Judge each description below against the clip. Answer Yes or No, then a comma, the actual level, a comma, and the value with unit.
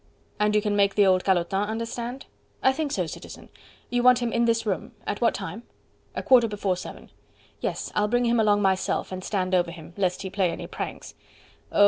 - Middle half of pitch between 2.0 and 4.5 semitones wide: Yes, average, 3.6 semitones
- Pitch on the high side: Yes, high, 210 Hz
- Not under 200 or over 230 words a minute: Yes, fast, 205 wpm